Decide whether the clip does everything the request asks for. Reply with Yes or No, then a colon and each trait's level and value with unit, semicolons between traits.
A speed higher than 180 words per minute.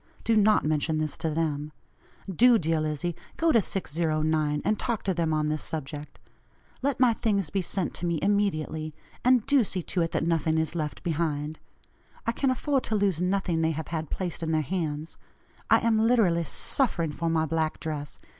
Yes: average, 190 wpm